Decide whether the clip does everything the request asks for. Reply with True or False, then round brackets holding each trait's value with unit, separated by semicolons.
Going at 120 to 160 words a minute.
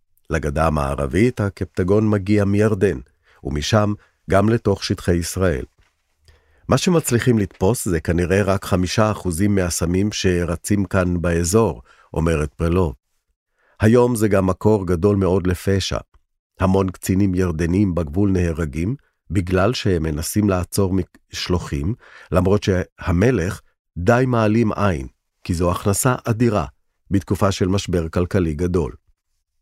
False (110 wpm)